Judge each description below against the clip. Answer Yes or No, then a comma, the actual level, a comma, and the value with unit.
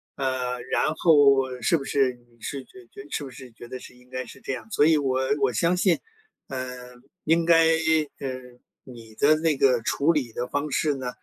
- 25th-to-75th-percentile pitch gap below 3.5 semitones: Yes, average, 2.9 semitones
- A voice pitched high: No, low, 135 Hz